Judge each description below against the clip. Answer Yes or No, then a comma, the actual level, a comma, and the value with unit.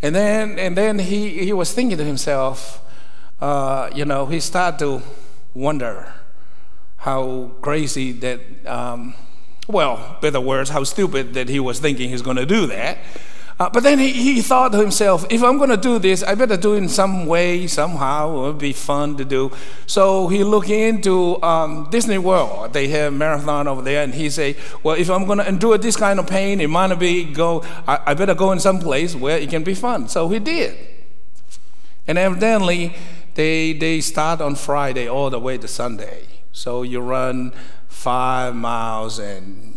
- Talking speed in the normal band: Yes, average, 190 wpm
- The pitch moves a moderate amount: No, wide, 6.2 semitones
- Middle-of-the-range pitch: Yes, medium, 155 Hz